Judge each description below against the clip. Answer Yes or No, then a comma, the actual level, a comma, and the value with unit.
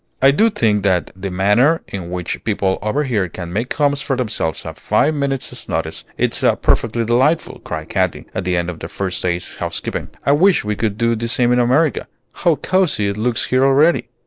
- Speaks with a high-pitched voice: No, low, 115 Hz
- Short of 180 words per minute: No, average, 200 wpm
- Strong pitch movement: Yes, wide, 6.6 semitones